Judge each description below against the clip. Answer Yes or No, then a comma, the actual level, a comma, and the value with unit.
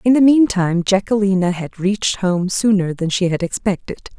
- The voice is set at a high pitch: Yes, high, 195 Hz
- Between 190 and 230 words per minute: No, average, 170 wpm